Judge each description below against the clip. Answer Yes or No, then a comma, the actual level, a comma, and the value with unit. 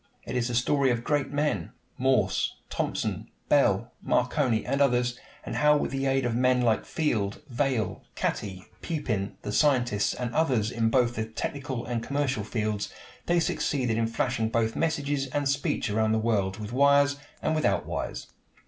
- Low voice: Yes, low, 125 Hz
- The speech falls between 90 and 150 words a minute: No, average, 165 wpm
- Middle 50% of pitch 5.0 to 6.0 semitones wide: No, average, 4.2 semitones